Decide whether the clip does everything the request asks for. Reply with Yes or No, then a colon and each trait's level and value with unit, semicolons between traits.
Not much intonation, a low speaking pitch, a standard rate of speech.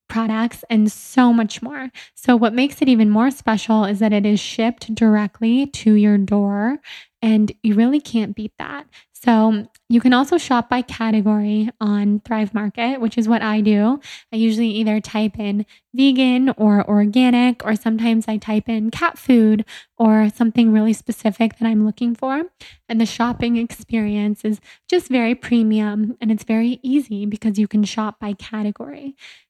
No: narrow, 2.1 semitones; high, 225 Hz; average, 170 wpm